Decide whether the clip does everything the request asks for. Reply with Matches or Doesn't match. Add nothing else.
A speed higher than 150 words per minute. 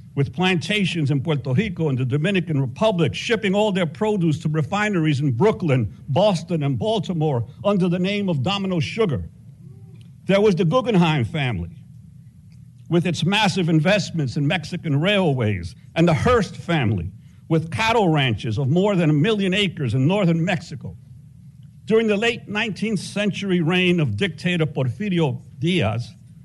Doesn't match